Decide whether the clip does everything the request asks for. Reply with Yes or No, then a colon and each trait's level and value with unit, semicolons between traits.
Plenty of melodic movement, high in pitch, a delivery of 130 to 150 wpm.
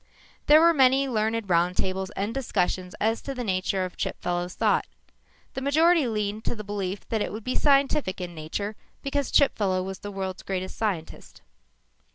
No: wide, 5.9 semitones; high, 205 Hz; average, 170 wpm